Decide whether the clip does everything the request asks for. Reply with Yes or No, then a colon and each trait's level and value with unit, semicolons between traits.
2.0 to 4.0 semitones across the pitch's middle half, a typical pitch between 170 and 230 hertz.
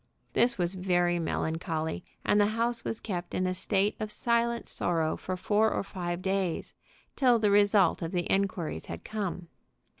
Yes: average, 3.4 semitones; high, 190 Hz